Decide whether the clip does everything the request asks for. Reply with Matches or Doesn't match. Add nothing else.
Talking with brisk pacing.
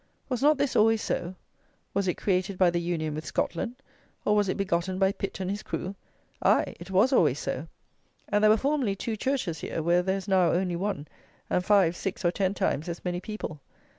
Matches